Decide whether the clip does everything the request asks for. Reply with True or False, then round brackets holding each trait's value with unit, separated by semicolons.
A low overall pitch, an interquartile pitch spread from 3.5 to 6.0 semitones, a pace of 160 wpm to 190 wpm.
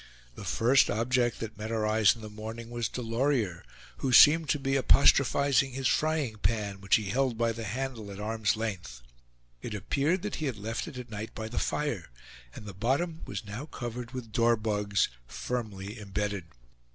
True (115 Hz; 3.9 semitones; 180 wpm)